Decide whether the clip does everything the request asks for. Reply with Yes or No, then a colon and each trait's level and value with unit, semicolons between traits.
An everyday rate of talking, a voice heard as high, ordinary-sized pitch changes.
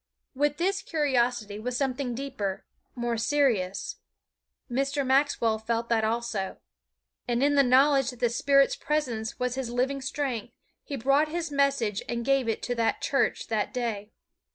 Yes: average, 155 wpm; very high, 250 Hz; average, 3.2 semitones